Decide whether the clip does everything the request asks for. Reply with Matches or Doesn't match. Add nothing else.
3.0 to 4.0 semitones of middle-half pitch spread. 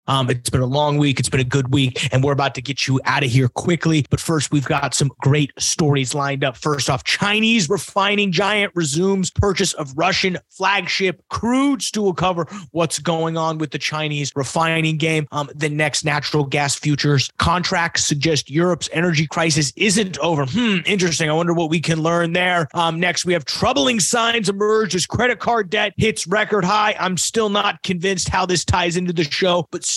Doesn't match